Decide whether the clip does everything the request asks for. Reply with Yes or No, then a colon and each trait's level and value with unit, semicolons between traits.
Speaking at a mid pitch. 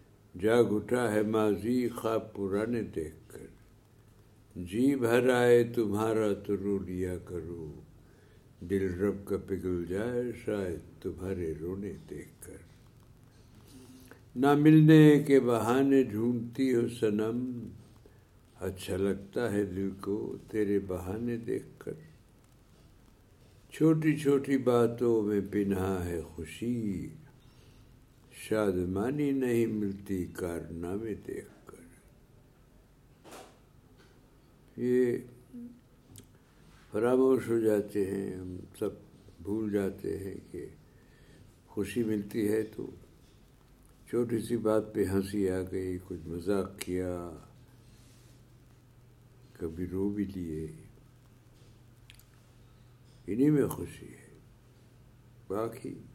No: low, 110 Hz